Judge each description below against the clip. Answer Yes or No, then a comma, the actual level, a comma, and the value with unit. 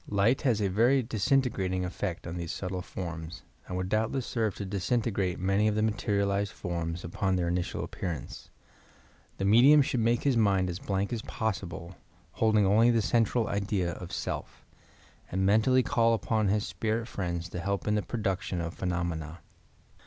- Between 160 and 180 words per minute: Yes, average, 175 wpm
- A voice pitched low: Yes, low, 100 Hz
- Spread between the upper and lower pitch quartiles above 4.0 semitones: No, average, 3.7 semitones